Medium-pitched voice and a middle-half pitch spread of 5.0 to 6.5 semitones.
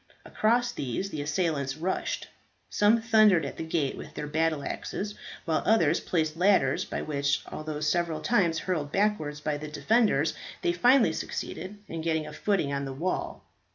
Yes: medium, 165 Hz; wide, 5.5 semitones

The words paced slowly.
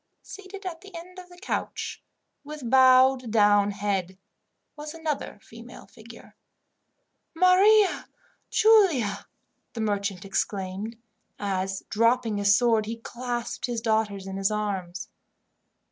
Yes: slow, 115 wpm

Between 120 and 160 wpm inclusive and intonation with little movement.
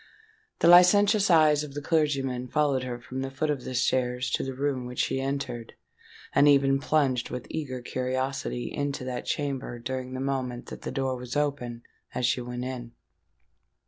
No: average, 175 wpm; narrow, 2.3 semitones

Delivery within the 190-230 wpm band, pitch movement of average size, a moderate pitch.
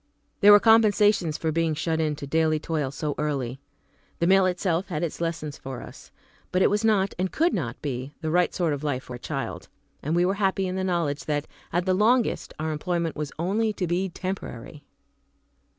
Yes: fast, 205 wpm; average, 4.0 semitones; medium, 170 Hz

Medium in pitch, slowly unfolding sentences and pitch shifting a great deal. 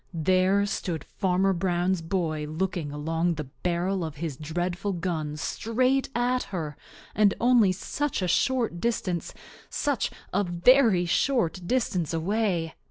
No: medium, 180 Hz; slow, 130 wpm; average, 4.2 semitones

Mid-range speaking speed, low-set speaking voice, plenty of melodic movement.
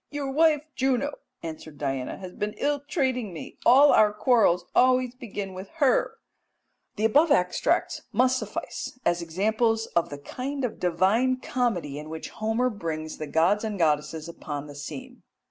No: average, 160 wpm; high, 215 Hz; wide, 7.5 semitones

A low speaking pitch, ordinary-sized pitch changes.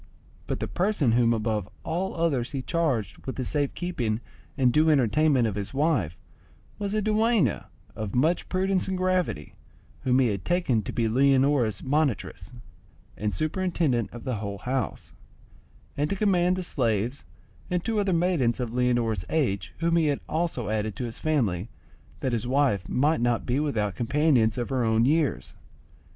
No: low, 130 Hz; wide, 6.5 semitones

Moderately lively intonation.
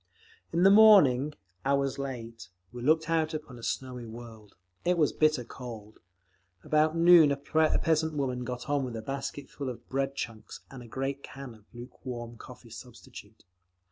Yes: average, 4.2 semitones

